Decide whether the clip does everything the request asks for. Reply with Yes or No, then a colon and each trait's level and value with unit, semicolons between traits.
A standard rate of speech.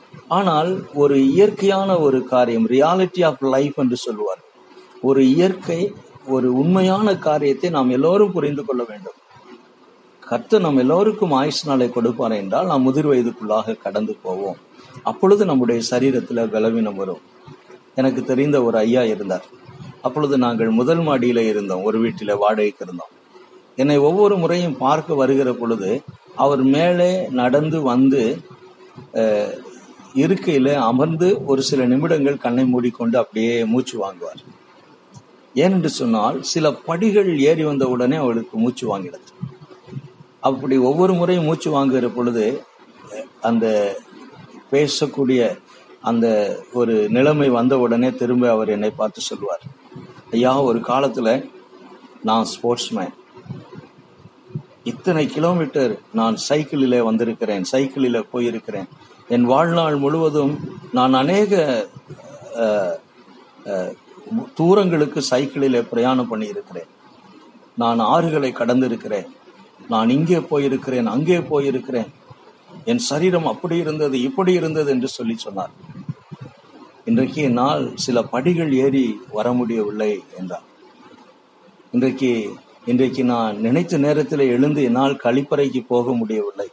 Yes: average, 105 wpm